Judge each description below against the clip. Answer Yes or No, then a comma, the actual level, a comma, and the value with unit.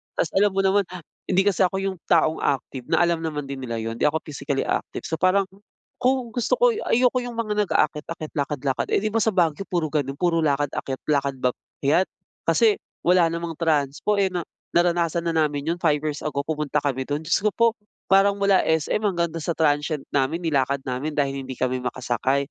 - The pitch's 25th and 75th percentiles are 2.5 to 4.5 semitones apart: No, average, 5.2 semitones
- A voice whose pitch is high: No, medium, 160 Hz